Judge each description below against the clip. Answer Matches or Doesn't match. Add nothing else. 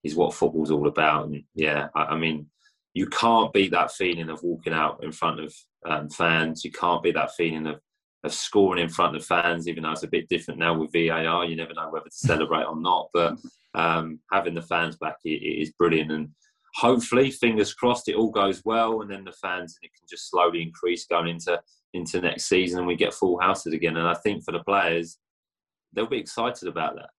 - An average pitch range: Doesn't match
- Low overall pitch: Matches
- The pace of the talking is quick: Matches